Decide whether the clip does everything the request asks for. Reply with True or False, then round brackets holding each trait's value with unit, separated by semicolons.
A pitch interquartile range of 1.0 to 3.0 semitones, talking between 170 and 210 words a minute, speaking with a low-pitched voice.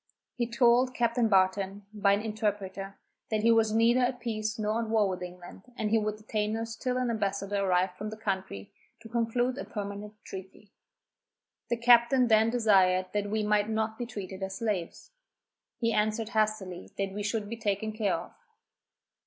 False (2.4 semitones; 175 wpm; 215 Hz)